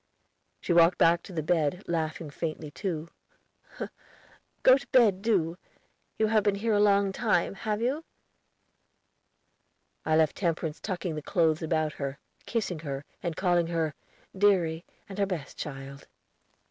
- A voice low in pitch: No, medium, 170 Hz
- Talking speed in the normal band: Yes, average, 145 wpm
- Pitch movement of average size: Yes, average, 4.2 semitones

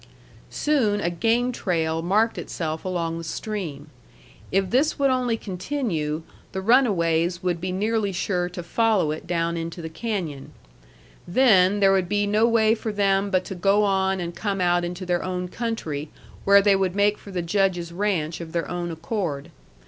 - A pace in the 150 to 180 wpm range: Yes, average, 175 wpm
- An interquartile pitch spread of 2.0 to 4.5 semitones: Yes, average, 3.6 semitones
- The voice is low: No, medium, 185 Hz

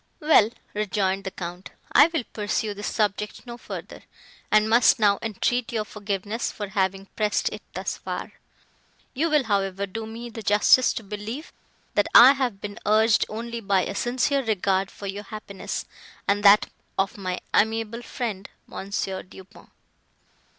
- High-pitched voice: Yes, high, 210 Hz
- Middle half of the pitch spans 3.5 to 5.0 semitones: No, average, 2.7 semitones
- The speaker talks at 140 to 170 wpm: Yes, average, 155 wpm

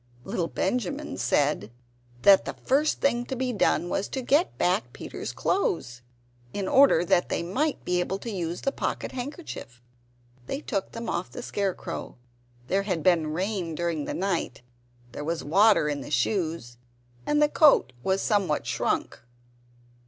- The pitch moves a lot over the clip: Yes, wide, 7.2 semitones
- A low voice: No, high, 190 Hz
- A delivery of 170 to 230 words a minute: No, average, 160 wpm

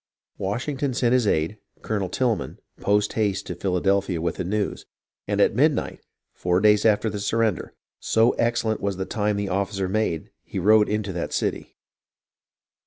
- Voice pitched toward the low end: Yes, low, 105 Hz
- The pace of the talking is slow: No, average, 160 wpm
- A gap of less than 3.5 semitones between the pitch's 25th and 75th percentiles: Yes, narrow, 2.5 semitones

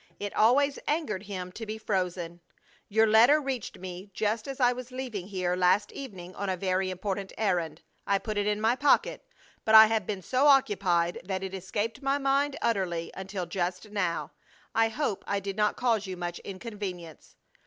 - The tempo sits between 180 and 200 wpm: Yes, average, 185 wpm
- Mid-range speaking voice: No, high, 205 Hz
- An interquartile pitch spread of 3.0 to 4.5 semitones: Yes, average, 3.7 semitones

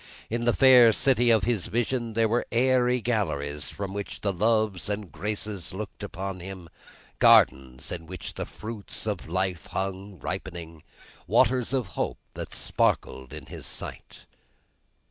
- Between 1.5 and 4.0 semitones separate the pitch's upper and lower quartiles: No, average, 4.4 semitones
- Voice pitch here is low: Yes, low, 100 Hz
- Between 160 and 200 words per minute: No, average, 145 wpm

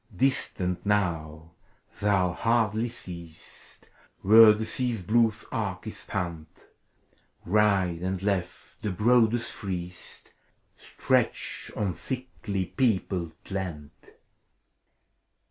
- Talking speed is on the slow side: Yes, slow, 95 wpm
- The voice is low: Yes, low, 100 Hz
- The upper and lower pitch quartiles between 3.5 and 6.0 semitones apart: Yes, average, 3.9 semitones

